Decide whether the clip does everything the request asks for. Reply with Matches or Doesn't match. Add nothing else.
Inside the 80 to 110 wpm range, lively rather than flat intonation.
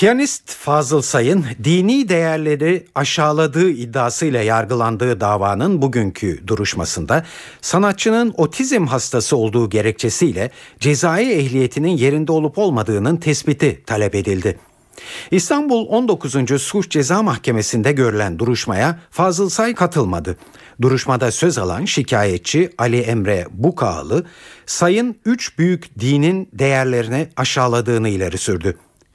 Matches